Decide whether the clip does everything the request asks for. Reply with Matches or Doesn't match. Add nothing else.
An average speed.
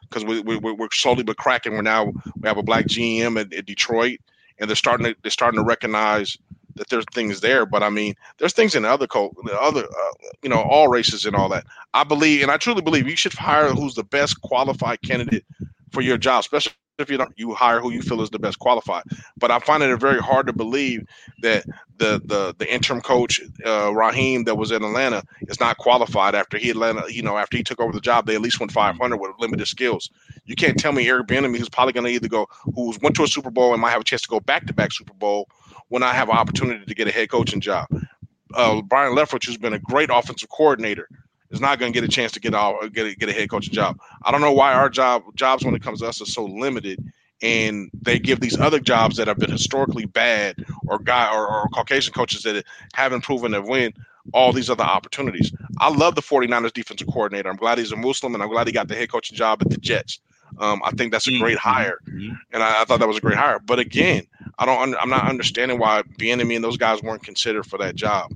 Doesn't match